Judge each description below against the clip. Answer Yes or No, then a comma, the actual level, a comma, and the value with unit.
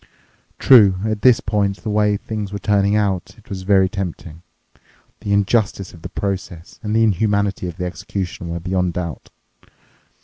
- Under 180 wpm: Yes, average, 165 wpm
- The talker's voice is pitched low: Yes, low, 100 Hz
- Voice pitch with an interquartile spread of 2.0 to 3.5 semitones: Yes, narrow, 2.4 semitones